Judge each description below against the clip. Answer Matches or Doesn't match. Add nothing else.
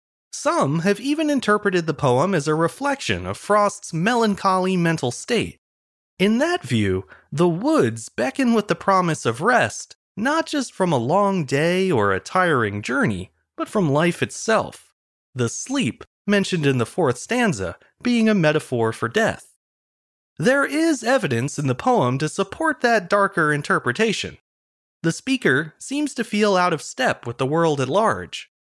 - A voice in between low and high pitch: Matches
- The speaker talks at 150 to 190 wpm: Matches